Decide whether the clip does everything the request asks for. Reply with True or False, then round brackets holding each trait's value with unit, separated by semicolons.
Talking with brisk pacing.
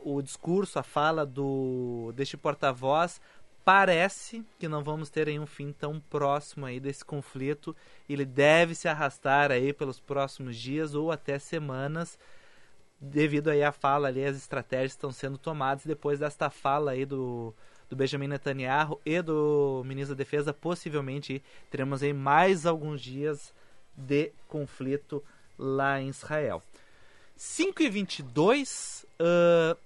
False (135 wpm)